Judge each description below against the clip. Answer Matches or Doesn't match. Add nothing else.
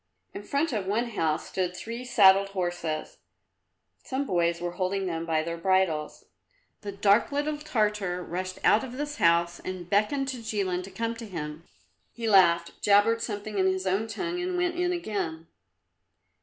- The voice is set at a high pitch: Matches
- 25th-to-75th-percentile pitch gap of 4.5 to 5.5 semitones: Matches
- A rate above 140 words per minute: Matches